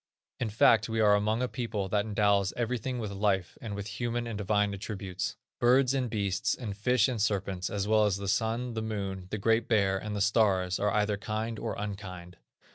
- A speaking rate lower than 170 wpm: No, average, 200 wpm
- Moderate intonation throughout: No, narrow, 2.3 semitones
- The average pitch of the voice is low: Yes, low, 105 Hz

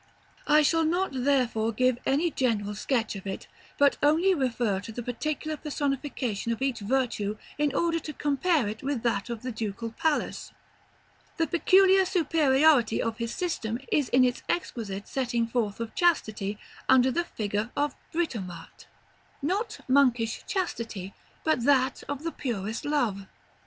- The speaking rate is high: No, average, 150 wpm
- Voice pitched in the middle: No, very high, 255 Hz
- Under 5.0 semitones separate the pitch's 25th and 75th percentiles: No, average, 5.3 semitones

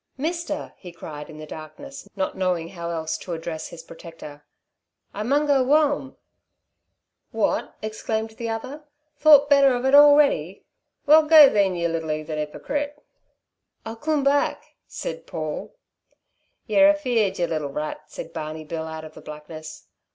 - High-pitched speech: Yes, high, 205 Hz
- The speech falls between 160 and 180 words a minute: No, average, 150 wpm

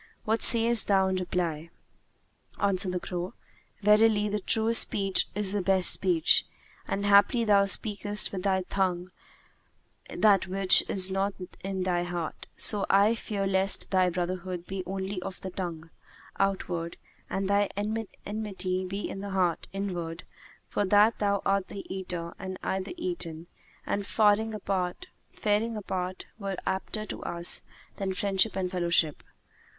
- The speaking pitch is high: Yes, high, 195 Hz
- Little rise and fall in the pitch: Yes, narrow, 2.0 semitones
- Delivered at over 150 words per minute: No, average, 145 wpm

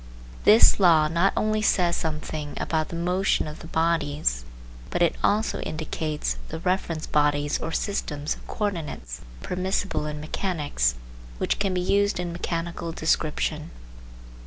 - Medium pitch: Yes, medium, 165 Hz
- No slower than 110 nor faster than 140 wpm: Yes, slow, 135 wpm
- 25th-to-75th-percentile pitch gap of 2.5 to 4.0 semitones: Yes, average, 3.4 semitones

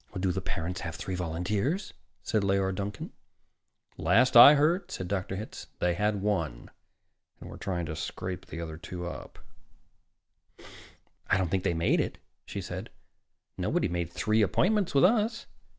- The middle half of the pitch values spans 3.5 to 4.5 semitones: Yes, average, 4.1 semitones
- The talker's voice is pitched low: Yes, very low, 95 Hz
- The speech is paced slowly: No, average, 150 wpm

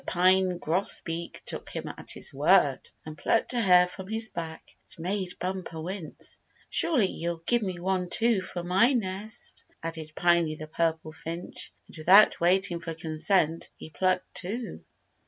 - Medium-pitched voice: Yes, medium, 180 Hz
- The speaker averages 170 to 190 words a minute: No, average, 155 wpm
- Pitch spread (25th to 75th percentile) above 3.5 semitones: No, average, 2.7 semitones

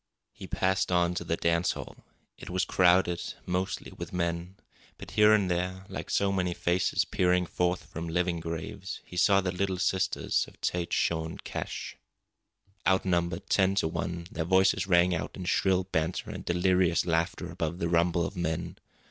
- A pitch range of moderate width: No, narrow, 1.7 semitones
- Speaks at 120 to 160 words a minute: No, average, 170 wpm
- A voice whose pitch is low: Yes, very low, 90 Hz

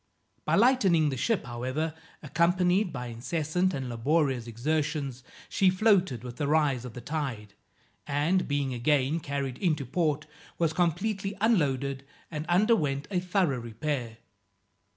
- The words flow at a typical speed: No, slow, 130 wpm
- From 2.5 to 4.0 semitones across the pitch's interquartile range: No, average, 5.3 semitones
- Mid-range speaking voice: Yes, medium, 150 Hz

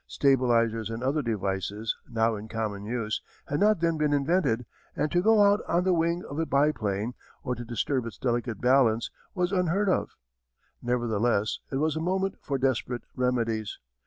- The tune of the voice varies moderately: No, wide, 6.1 semitones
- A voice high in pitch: No, low, 125 Hz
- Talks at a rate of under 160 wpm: No, average, 170 wpm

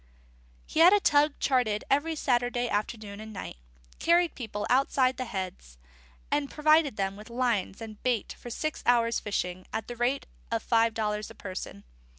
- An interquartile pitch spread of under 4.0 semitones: No, average, 4.5 semitones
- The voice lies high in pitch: Yes, high, 235 Hz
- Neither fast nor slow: Yes, average, 170 wpm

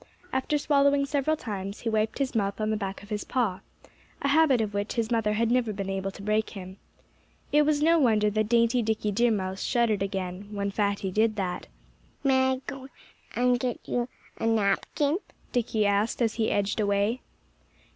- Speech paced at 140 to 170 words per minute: No, average, 185 wpm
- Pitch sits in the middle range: No, high, 220 Hz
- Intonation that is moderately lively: Yes, average, 3.9 semitones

